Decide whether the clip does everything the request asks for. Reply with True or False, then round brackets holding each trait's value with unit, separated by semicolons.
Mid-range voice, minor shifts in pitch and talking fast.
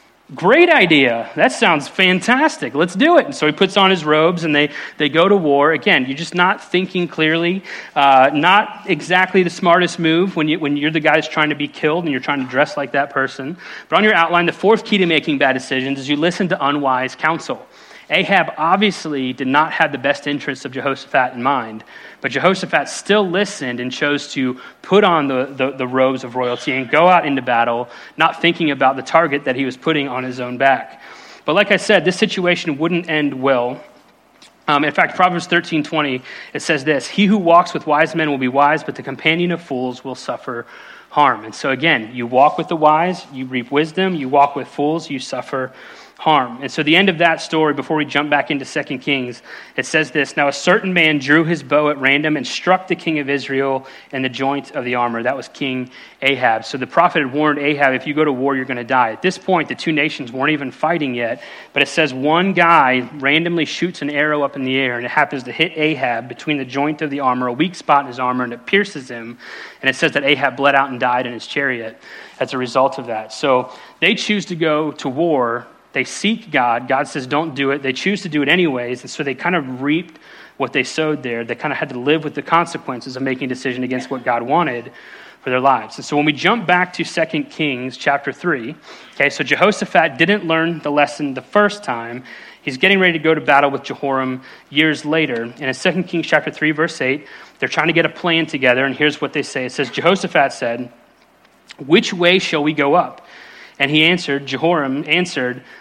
False (145 Hz; 3.9 semitones; 230 wpm)